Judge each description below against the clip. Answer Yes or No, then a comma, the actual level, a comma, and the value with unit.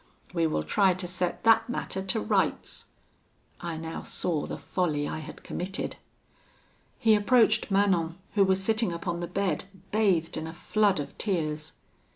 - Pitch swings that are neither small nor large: Yes, average, 3.7 semitones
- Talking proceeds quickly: No, average, 160 wpm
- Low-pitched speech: No, medium, 180 Hz